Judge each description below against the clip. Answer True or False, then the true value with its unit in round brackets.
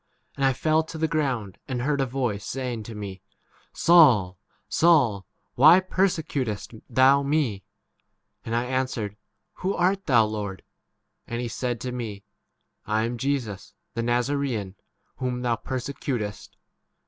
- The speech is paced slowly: False (150 wpm)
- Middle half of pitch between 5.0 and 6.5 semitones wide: False (4.4 semitones)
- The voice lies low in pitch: True (125 Hz)